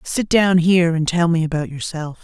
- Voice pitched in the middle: Yes, medium, 170 Hz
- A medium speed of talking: No, fast, 215 wpm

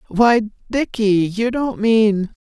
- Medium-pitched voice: No, high, 215 Hz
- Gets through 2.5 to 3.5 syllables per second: Yes, 2.8 syllables/s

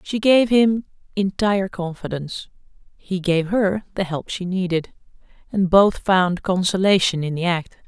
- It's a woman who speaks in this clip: Yes, female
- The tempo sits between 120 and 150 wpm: Yes, average, 145 wpm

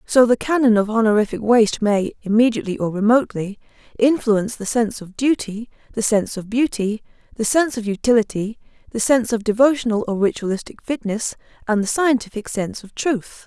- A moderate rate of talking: Yes, average, 160 wpm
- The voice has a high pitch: Yes, high, 225 Hz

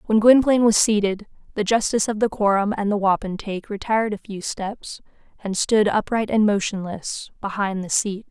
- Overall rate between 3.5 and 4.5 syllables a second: No, 5.3 syllables/s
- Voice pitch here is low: No, high, 210 Hz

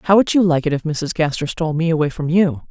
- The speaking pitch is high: No, medium, 160 Hz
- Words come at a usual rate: No, fast, 290 wpm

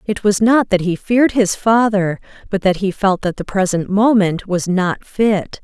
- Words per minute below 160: No, average, 200 wpm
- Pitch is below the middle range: No, high, 200 Hz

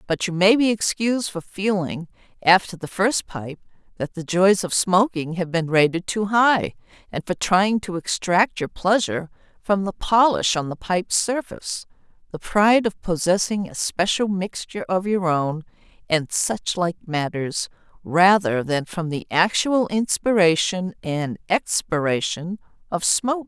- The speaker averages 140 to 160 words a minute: Yes, average, 150 wpm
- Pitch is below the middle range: No, medium, 185 Hz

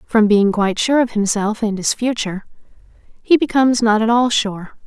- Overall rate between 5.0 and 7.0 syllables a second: Yes, 5.2 syllables/s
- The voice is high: Yes, high, 220 Hz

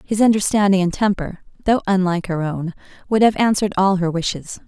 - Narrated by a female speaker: Yes, female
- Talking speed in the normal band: Yes, average, 180 wpm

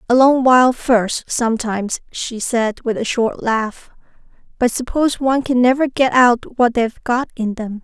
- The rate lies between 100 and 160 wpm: No, average, 175 wpm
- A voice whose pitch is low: No, high, 240 Hz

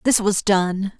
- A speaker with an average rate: Yes, average, 180 wpm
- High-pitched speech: Yes, high, 200 Hz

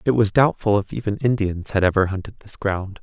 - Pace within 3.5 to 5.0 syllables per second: No, 5.5 syllables/s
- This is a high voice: No, low, 105 Hz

